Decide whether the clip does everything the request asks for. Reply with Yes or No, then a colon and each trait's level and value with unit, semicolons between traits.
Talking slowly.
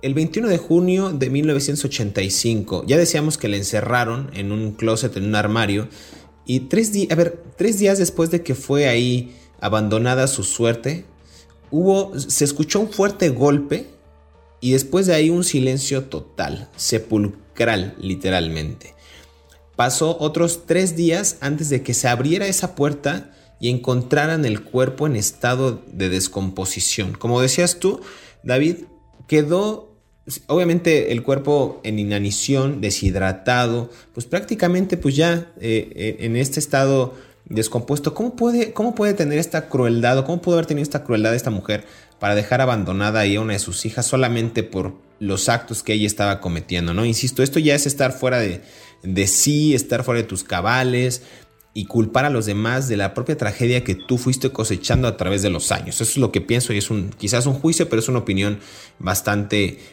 No: average, 170 wpm